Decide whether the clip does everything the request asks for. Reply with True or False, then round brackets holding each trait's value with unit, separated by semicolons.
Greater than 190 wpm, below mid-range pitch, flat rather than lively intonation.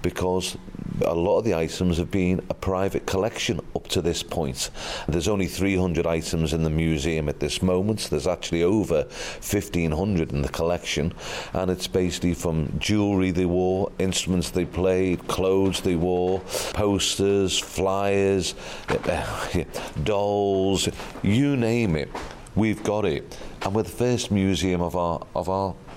False (150 wpm; 90 Hz; 2.2 semitones)